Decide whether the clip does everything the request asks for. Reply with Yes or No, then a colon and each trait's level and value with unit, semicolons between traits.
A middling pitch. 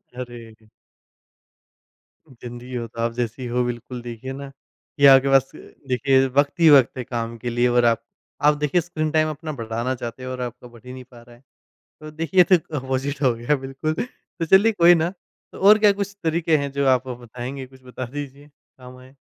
No: low, 130 Hz